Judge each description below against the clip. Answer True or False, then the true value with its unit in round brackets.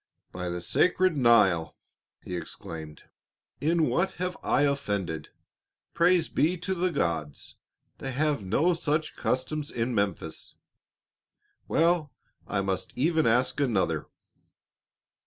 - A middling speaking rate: False (115 wpm)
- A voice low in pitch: True (130 Hz)